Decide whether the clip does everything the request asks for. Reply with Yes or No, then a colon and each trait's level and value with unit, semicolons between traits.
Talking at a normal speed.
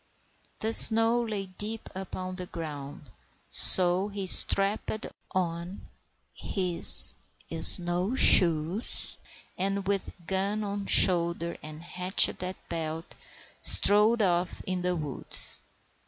No: slow, 105 wpm